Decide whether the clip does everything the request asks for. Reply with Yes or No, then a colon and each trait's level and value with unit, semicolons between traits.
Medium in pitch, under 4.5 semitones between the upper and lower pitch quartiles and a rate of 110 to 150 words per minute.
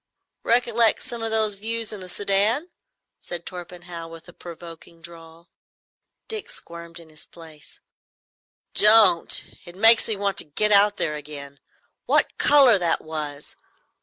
No: medium, 180 Hz; average, 4.9 semitones; average, 140 wpm